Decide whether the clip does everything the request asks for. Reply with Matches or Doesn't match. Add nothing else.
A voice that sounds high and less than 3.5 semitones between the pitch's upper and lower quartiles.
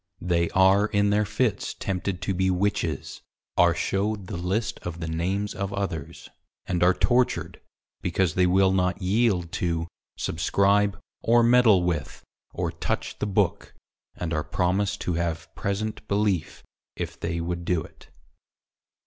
Doesn't match